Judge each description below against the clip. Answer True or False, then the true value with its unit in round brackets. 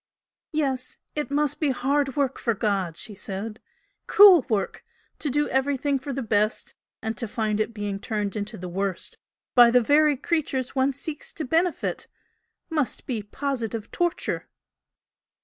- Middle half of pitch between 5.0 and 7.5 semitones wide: True (5.3 semitones)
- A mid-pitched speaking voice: False (255 Hz)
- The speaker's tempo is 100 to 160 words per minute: True (150 wpm)